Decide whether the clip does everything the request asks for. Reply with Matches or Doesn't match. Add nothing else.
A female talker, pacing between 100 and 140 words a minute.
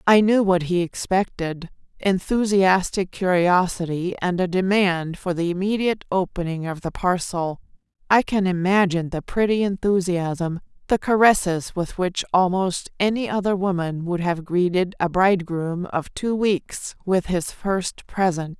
Matches